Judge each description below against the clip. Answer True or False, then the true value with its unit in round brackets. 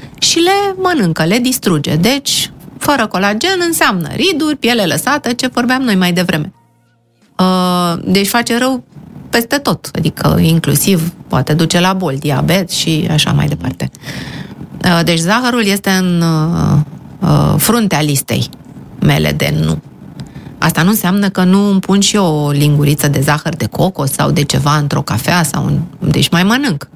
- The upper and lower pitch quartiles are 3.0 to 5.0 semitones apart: False (5.4 semitones)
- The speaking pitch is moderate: True (175 Hz)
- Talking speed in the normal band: True (160 wpm)